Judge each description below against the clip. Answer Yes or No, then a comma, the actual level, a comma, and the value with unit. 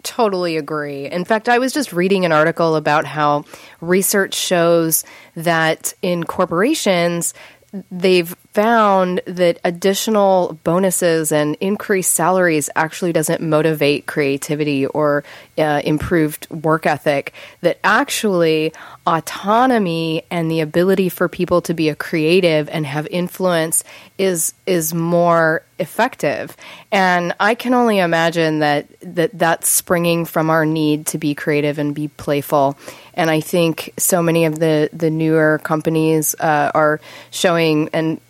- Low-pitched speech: No, medium, 165 Hz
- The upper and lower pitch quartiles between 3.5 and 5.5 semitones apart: No, average, 2.8 semitones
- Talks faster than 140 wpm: No, slow, 135 wpm